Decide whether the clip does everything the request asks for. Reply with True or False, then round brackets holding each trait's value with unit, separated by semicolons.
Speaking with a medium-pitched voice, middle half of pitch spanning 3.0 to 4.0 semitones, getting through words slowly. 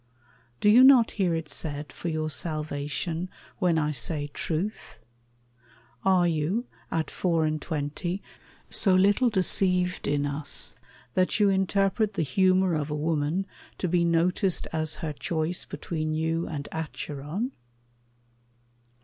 True (165 Hz; 3.5 semitones; 130 wpm)